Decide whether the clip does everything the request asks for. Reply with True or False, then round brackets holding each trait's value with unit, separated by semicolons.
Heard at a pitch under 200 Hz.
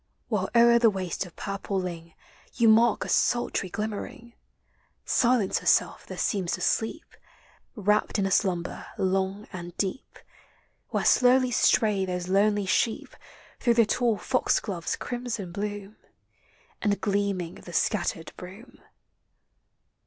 False (205 Hz)